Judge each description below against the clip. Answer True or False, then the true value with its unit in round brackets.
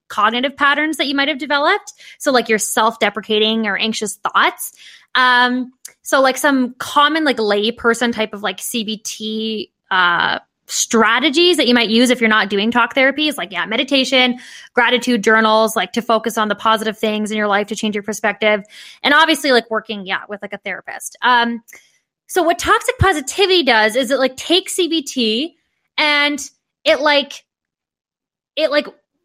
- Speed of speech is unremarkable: True (165 wpm)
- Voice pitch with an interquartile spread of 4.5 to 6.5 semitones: True (5.0 semitones)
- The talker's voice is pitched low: False (245 Hz)